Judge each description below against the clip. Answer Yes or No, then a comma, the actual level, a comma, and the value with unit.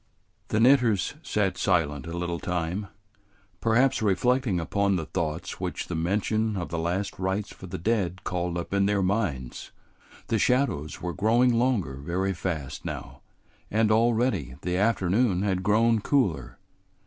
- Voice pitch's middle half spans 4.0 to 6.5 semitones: Yes, average, 4.3 semitones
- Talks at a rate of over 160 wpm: No, average, 150 wpm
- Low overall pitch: Yes, very low, 95 Hz